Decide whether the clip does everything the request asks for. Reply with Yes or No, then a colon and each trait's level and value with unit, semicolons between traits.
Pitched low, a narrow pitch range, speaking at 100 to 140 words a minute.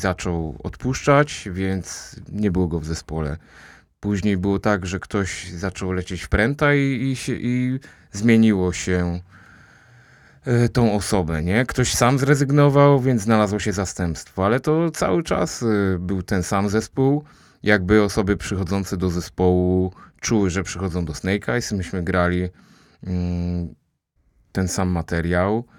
No: very low, 95 Hz; average, 3.9 semitones; average, 130 wpm